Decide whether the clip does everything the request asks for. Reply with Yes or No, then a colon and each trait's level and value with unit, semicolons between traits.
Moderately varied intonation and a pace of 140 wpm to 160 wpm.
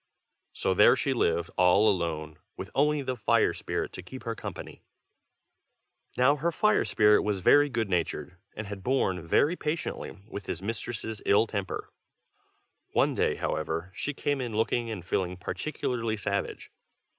No: wide, 5.7 semitones; average, 155 wpm